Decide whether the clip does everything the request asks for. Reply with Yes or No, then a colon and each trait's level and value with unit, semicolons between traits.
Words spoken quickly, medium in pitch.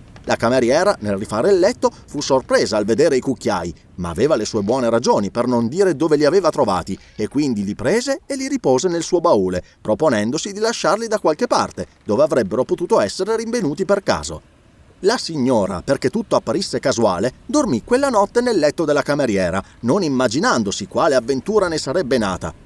Yes: fast, 180 wpm; medium, 175 Hz